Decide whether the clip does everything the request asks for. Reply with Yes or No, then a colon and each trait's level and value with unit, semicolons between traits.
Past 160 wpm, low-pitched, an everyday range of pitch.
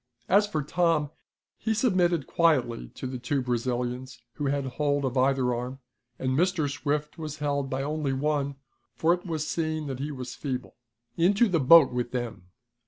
No: average, 170 wpm; medium, 145 Hz; average, 3.7 semitones